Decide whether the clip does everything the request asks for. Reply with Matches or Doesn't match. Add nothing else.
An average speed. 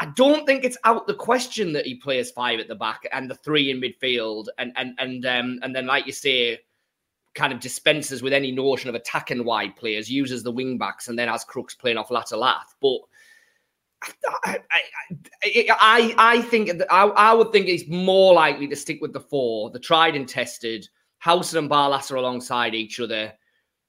Matches